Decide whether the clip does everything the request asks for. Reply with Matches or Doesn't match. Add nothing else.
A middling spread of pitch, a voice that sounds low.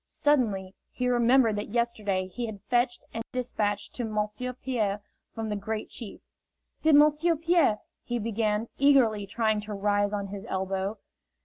Doesn't match